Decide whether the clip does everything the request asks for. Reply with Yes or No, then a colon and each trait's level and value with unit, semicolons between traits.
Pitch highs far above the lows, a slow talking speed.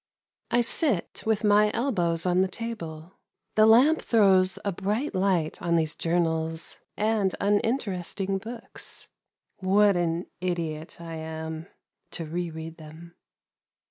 No: average, 4.2 semitones; slow, 125 wpm